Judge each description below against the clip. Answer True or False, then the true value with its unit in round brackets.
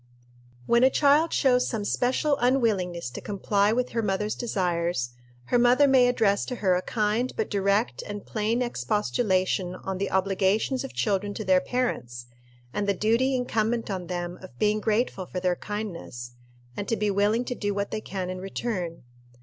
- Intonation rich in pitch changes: False (4.2 semitones)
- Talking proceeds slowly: False (175 wpm)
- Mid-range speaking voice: False (210 Hz)